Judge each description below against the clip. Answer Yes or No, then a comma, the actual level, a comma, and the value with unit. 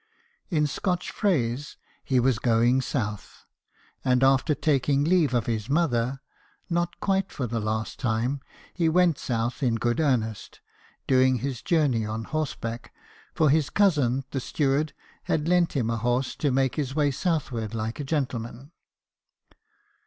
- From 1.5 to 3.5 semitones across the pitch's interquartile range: No, average, 4.5 semitones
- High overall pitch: No, low, 135 Hz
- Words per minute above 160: No, average, 145 wpm